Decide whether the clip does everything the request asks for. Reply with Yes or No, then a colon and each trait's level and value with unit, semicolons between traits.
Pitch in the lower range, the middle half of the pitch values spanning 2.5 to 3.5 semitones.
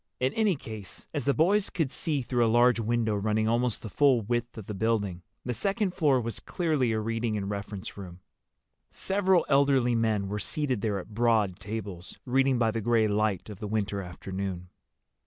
No: low, 115 Hz; average, 4.2 semitones